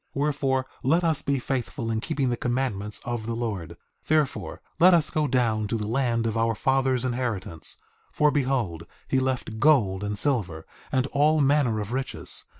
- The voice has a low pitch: Yes, low, 125 Hz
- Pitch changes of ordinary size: Yes, average, 4.0 semitones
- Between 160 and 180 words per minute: Yes, average, 175 wpm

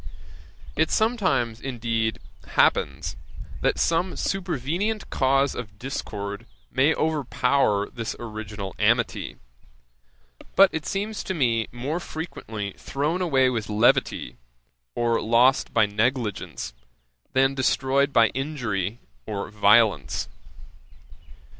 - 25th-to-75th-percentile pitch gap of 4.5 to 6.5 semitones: Yes, average, 5.3 semitones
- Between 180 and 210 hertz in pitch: No, low, 125 Hz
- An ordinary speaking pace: No, slow, 100 wpm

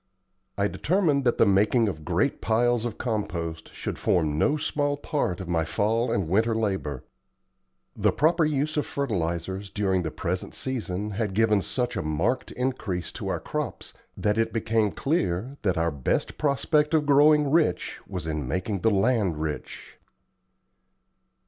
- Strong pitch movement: Yes, wide, 6.6 semitones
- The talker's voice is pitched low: Yes, low, 105 Hz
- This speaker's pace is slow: No, average, 155 wpm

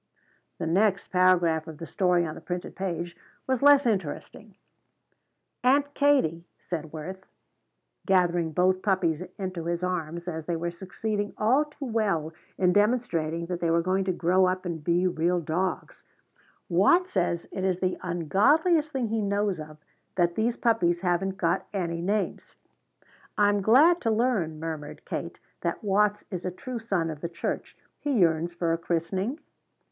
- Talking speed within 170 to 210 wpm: No, average, 160 wpm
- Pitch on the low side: No, medium, 185 Hz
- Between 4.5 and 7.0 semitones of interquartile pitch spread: No, average, 3.8 semitones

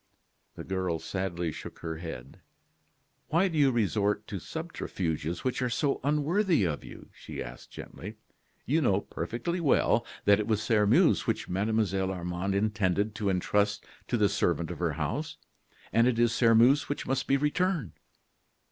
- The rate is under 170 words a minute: Yes, average, 155 wpm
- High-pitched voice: No, low, 105 Hz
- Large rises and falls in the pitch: Yes, wide, 5.9 semitones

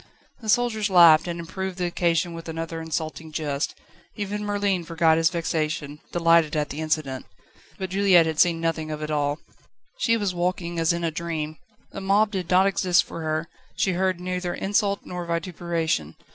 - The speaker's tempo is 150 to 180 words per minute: Yes, average, 175 wpm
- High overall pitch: No, medium, 170 Hz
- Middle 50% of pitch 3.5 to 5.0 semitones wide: No, average, 2.8 semitones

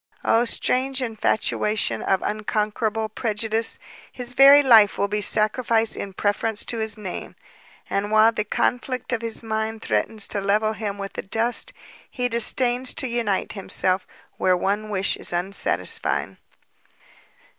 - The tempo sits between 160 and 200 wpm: No, average, 140 wpm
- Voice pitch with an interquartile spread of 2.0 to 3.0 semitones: Yes, narrow, 2.4 semitones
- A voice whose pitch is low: No, high, 220 Hz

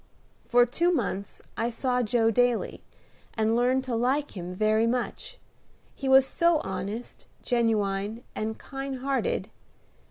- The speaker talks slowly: Yes, slow, 130 wpm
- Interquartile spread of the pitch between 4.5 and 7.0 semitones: No, average, 3.4 semitones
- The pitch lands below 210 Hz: No, high, 240 Hz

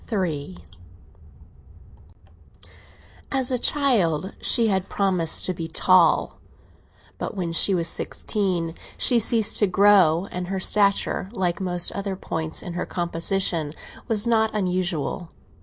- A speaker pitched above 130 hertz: Yes, medium, 185 Hz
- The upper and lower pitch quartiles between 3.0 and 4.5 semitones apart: Yes, average, 3.4 semitones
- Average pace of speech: No, slow, 125 wpm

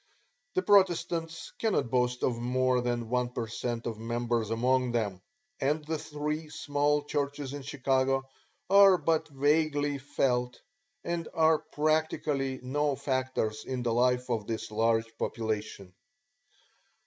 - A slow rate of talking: Yes, slow, 130 wpm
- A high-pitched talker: No, low, 130 Hz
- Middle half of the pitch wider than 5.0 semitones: No, average, 3.8 semitones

